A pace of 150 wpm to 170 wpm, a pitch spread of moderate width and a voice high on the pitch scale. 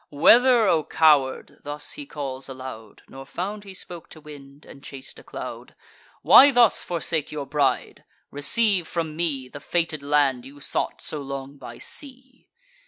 No: average, 160 wpm; average, 4.4 semitones; medium, 150 Hz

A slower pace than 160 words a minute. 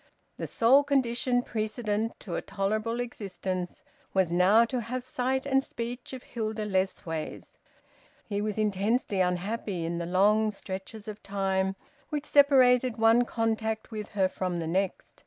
Yes: average, 145 wpm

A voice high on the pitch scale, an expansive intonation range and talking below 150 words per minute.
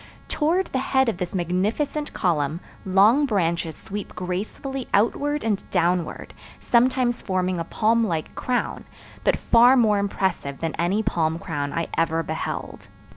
Yes: high, 195 Hz; wide, 6.2 semitones; average, 140 wpm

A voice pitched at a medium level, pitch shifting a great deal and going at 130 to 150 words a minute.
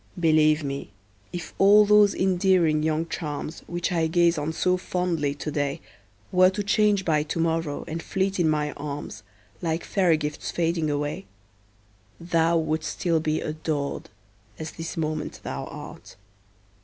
No: medium, 160 Hz; average, 2.7 semitones; average, 145 wpm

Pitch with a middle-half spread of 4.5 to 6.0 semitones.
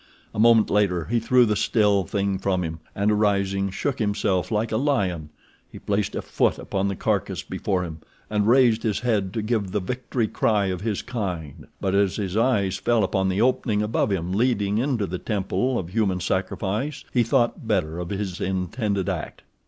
No: average, 3.0 semitones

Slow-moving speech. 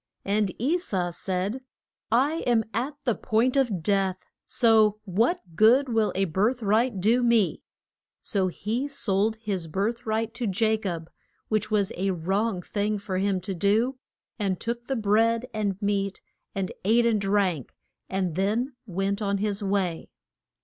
No: average, 155 wpm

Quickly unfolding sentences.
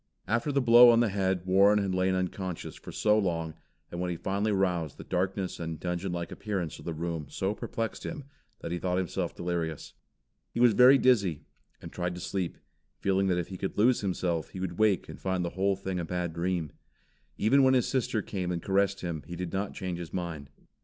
Yes: fast, 215 wpm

